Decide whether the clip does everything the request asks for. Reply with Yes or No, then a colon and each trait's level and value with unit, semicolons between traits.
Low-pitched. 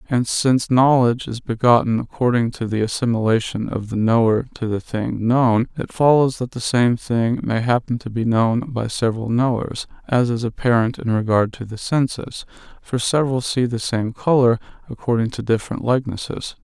Yes: low, 120 Hz